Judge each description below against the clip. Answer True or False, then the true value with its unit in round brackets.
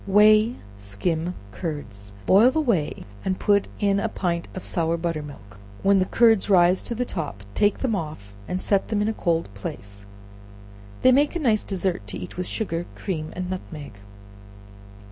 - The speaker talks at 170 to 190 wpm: True (175 wpm)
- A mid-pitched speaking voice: True (180 Hz)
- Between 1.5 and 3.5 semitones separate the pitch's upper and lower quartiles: False (5.3 semitones)